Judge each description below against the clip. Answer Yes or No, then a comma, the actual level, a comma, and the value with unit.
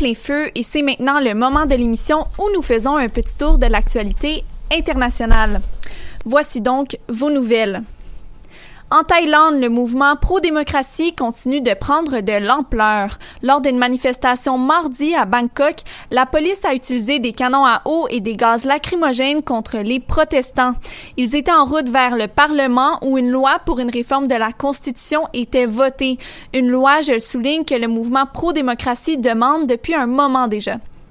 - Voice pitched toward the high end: Yes, very high, 265 Hz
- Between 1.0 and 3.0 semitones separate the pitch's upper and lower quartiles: No, average, 3.4 semitones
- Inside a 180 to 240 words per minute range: No, average, 165 wpm